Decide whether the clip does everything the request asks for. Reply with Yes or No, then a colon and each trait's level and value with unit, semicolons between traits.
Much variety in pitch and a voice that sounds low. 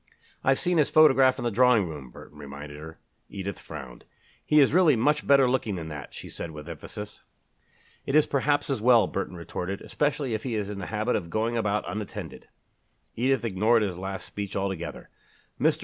Yes: wide, 6.7 semitones; low, 105 Hz